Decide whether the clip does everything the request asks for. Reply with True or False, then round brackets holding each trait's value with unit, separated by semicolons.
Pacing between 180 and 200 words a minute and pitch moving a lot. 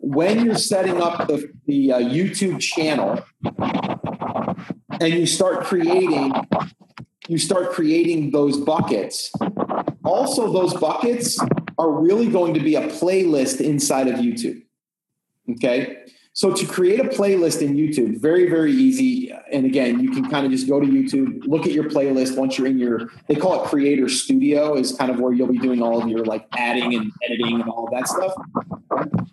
False (170 wpm; 6.5 semitones)